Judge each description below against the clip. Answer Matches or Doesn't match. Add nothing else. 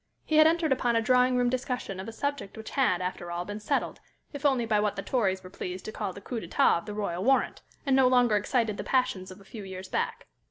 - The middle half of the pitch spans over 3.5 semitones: Matches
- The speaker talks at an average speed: Doesn't match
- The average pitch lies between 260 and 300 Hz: Doesn't match